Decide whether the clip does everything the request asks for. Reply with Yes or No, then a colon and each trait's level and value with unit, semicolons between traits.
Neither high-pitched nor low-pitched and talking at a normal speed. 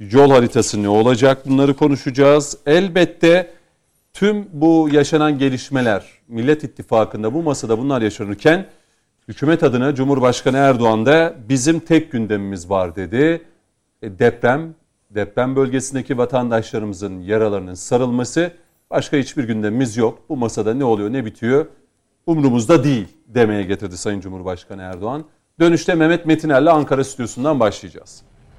No: low, 130 Hz; average, 120 wpm